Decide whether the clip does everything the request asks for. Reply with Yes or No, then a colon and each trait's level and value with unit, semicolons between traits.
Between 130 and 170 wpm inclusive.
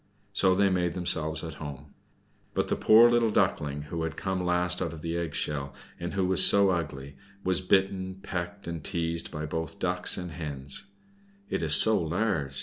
No: average, 185 wpm